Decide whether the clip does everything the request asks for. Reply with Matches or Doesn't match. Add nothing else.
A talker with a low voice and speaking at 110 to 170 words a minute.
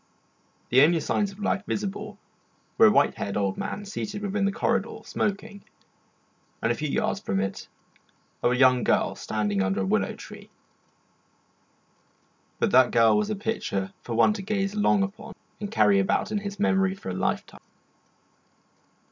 Doesn't match